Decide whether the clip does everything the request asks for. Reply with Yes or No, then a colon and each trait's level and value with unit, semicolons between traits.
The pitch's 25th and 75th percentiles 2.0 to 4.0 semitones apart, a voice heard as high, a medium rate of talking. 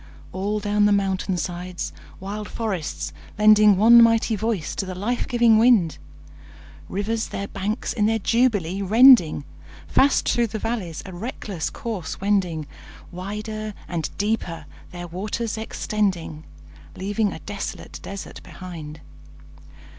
No: average, 3.3 semitones; high, 205 Hz; slow, 125 wpm